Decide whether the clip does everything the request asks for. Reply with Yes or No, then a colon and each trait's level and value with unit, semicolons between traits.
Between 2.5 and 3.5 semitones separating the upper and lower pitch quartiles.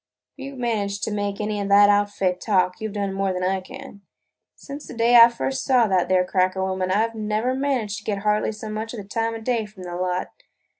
Yes: average, 2.9 semitones